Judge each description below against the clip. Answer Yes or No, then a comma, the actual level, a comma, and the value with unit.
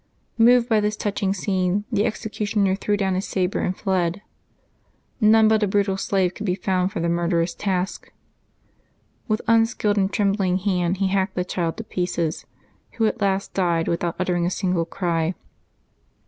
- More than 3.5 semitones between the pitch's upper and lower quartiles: No, narrow, 2.5 semitones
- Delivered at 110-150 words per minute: No, average, 165 wpm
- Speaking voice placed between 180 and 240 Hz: Yes, high, 190 Hz